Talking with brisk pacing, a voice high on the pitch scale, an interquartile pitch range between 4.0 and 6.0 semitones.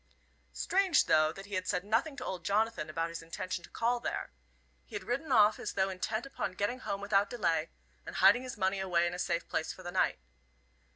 Yes: fast, 220 wpm; high, 195 Hz; average, 4.6 semitones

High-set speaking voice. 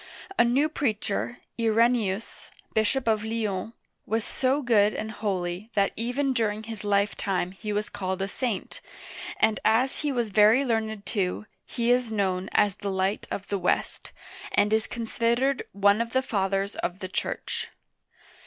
Yes: high, 215 Hz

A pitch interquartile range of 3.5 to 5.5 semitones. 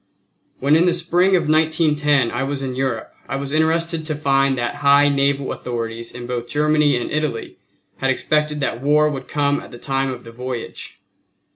No: average, 2.9 semitones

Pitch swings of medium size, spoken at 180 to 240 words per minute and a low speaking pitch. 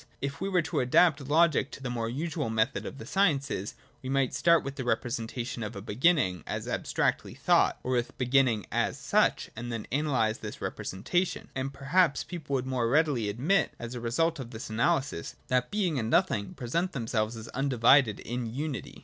Yes: average, 4.2 semitones; average, 190 wpm; low, 130 Hz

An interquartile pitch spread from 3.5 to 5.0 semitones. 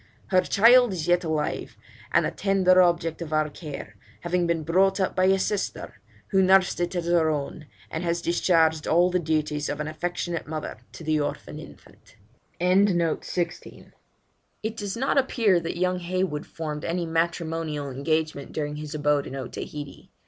No: average, 3.1 semitones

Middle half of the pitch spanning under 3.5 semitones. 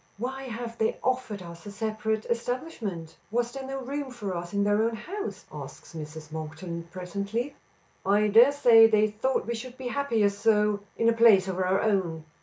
No: average, 4.2 semitones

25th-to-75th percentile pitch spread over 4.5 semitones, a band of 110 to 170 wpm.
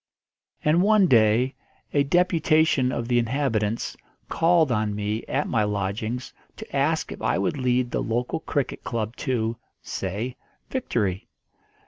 Yes: average, 4.9 semitones; slow, 135 wpm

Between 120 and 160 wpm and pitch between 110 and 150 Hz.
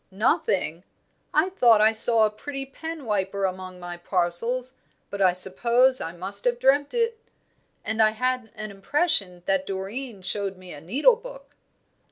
No: average, 155 wpm; high, 215 Hz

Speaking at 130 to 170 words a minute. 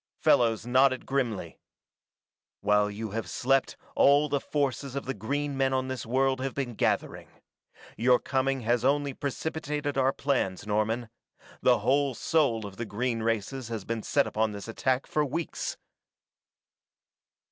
Yes: average, 145 wpm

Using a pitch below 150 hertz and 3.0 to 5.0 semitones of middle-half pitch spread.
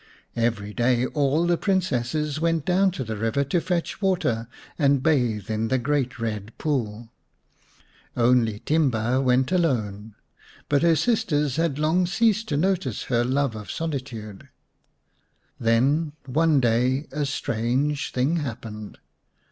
No: low, 135 Hz; wide, 5.5 semitones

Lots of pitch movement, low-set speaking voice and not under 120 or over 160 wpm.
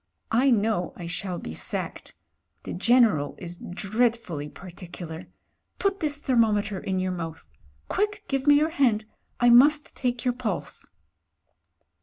No: wide, 6.4 semitones; high, 220 Hz; average, 145 wpm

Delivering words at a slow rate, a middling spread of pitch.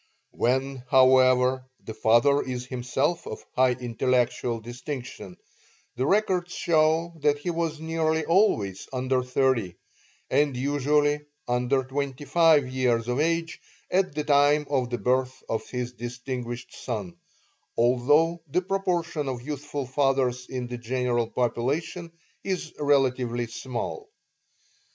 Yes: slow, 125 wpm; average, 3.4 semitones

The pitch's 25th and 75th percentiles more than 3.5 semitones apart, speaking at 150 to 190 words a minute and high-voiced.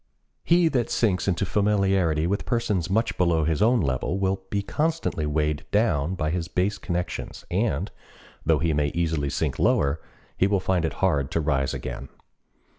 No: average, 4.5 semitones; average, 170 wpm; very low, 90 Hz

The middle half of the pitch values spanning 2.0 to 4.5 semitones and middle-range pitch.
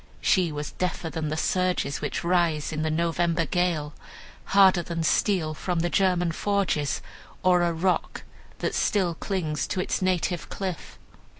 Yes: narrow, 2.5 semitones; medium, 175 Hz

